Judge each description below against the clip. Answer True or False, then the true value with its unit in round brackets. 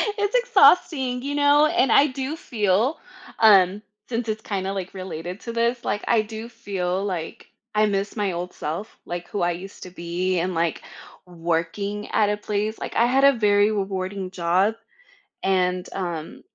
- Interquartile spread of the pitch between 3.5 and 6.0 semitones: True (4.3 semitones)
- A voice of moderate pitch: False (205 Hz)